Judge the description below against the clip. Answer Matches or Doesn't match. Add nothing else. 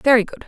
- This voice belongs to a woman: Matches